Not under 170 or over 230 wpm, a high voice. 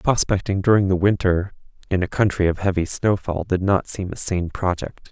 No: average, 190 wpm; very low, 95 Hz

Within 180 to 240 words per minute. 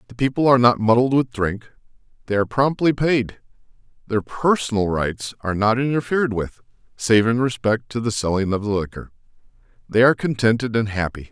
No: average, 165 wpm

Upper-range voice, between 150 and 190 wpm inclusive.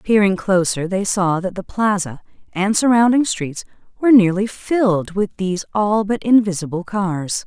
Yes: high, 200 Hz; average, 155 wpm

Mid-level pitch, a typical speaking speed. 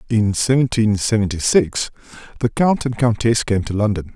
No: low, 110 Hz; average, 160 wpm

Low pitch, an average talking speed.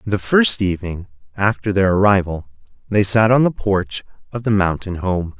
Yes: low, 100 Hz; average, 165 wpm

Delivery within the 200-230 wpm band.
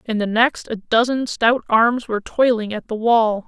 Yes: fast, 205 wpm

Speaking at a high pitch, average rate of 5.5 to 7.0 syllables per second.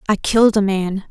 Yes: high, 200 Hz; 5.6 syllables/s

